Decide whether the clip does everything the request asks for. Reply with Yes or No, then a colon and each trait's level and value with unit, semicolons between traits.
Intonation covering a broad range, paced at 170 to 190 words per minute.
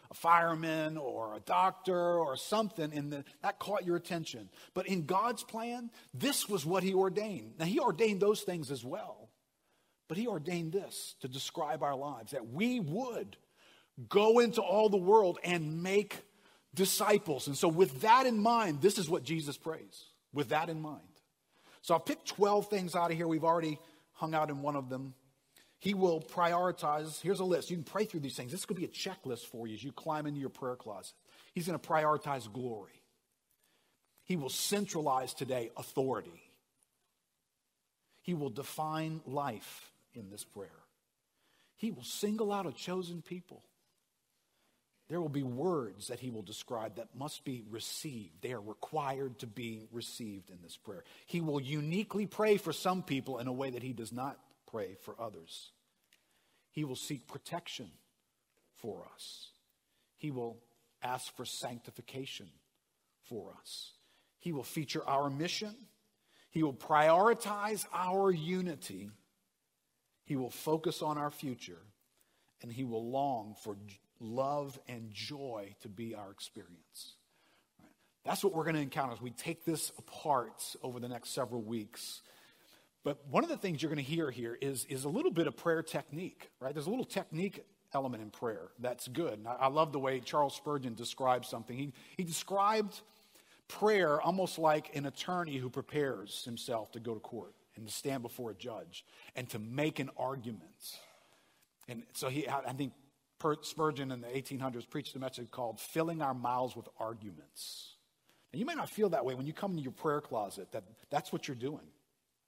Yes: wide, 5.9 semitones; average, 175 wpm